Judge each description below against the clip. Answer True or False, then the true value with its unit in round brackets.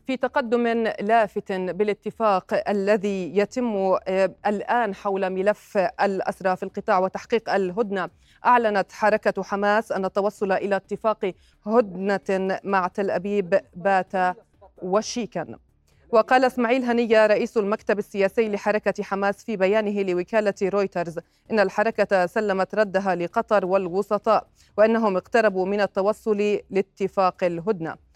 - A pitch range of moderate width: False (2.2 semitones)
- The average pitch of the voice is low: False (200 Hz)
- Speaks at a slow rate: False (110 wpm)